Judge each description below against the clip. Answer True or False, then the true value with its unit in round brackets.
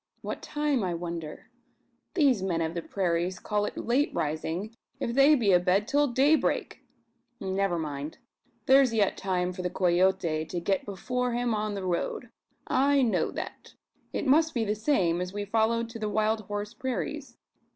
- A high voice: True (205 Hz)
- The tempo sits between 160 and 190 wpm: True (170 wpm)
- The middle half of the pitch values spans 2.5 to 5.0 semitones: False (5.5 semitones)